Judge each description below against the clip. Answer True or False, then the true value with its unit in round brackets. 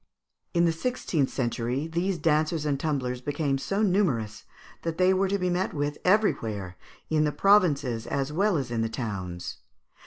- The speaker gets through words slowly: False (165 wpm)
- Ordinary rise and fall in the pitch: False (6.4 semitones)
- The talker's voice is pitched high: False (150 Hz)